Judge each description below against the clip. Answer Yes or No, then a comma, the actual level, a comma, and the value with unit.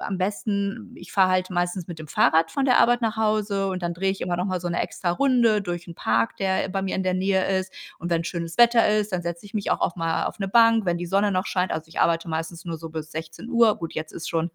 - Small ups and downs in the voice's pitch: No, average, 3.4 semitones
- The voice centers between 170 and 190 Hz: Yes, medium, 185 Hz